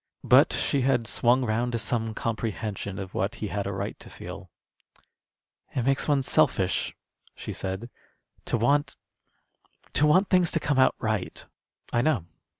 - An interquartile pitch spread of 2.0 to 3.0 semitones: No, average, 4.1 semitones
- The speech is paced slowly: No, average, 155 wpm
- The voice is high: No, low, 120 Hz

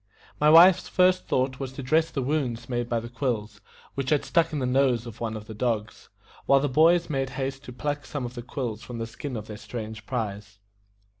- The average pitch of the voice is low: Yes, low, 125 Hz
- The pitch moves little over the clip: No, average, 4.0 semitones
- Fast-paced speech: Yes, fast, 225 wpm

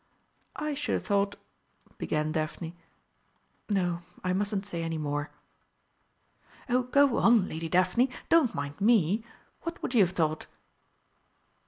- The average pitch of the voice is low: No, high, 190 Hz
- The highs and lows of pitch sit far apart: Yes, wide, 6.6 semitones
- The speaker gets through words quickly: No, slow, 135 wpm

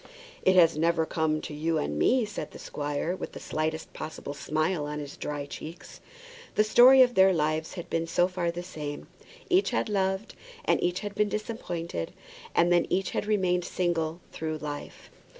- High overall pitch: No, medium, 170 Hz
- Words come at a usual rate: Yes, average, 185 wpm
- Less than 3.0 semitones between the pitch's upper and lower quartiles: No, average, 3.5 semitones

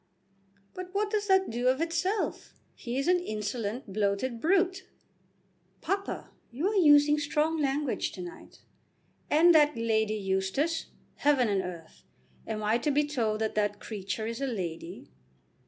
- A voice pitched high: Yes, very high, 265 Hz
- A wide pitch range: Yes, wide, 7.5 semitones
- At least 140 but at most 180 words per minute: Yes, average, 150 wpm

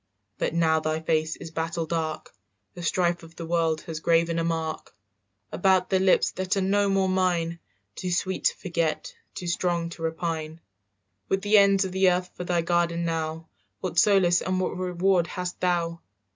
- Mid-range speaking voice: Yes, medium, 170 Hz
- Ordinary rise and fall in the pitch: No, narrow, 2.1 semitones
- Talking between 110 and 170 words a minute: No, average, 180 wpm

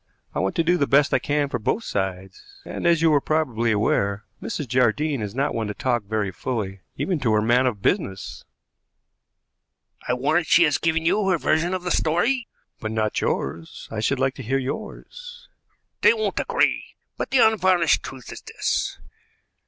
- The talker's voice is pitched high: No, low, 135 Hz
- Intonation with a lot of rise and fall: Yes, wide, 7.3 semitones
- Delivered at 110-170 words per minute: No, average, 185 wpm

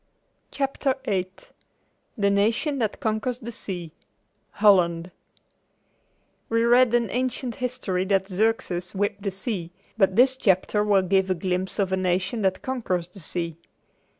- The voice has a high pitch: Yes, high, 200 Hz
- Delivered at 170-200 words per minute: No, average, 140 wpm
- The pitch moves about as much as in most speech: Yes, average, 4.0 semitones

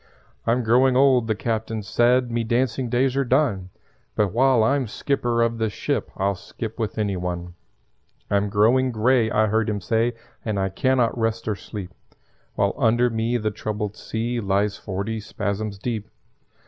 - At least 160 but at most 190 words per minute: Yes, average, 170 wpm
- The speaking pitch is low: Yes, low, 110 Hz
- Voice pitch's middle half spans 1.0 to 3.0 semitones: Yes, average, 2.7 semitones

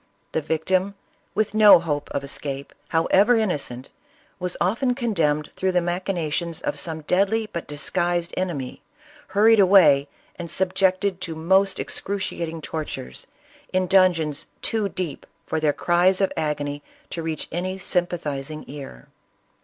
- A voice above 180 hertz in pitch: No, medium, 175 Hz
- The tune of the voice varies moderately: Yes, average, 3.9 semitones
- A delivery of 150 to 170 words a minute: No, slow, 135 wpm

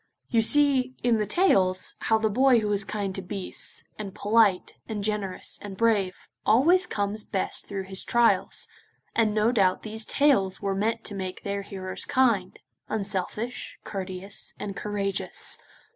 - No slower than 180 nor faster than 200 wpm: No, average, 155 wpm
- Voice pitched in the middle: No, high, 210 Hz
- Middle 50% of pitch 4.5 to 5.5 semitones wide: No, average, 2.8 semitones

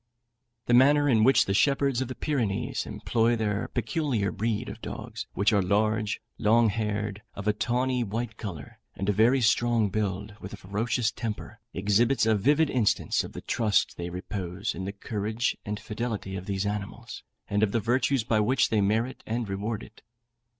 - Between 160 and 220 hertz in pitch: No, low, 110 Hz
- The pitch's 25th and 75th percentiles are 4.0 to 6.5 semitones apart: No, average, 2.9 semitones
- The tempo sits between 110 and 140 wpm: No, average, 180 wpm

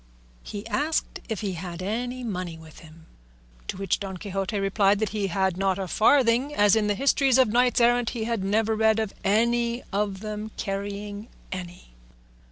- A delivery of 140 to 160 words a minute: No, average, 175 wpm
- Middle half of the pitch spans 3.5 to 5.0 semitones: No, average, 3.0 semitones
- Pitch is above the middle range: Yes, high, 210 Hz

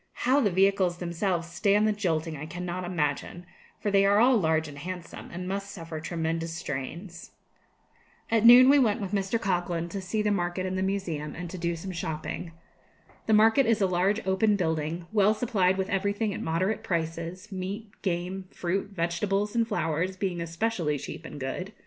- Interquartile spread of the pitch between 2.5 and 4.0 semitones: Yes, average, 3.3 semitones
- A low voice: No, medium, 185 Hz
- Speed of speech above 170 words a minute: Yes, average, 180 wpm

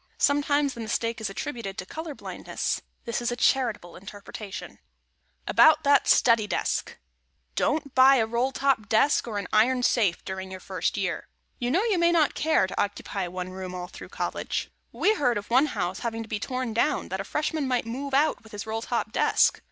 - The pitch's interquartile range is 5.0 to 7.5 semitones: Yes, average, 5.3 semitones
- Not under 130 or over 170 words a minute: No, average, 200 wpm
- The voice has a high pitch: Yes, high, 235 Hz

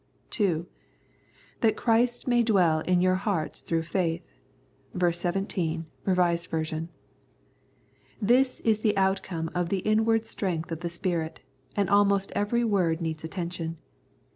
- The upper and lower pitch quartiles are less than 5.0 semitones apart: Yes, average, 3.8 semitones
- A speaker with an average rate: No, slow, 130 wpm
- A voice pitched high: No, medium, 180 Hz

